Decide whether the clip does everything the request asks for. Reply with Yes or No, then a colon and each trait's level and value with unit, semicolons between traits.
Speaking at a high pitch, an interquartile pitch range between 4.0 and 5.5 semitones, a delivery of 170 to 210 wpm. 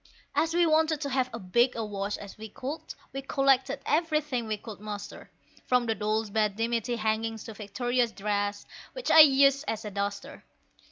Yes: high, 230 Hz; average, 4.4 semitones; average, 180 wpm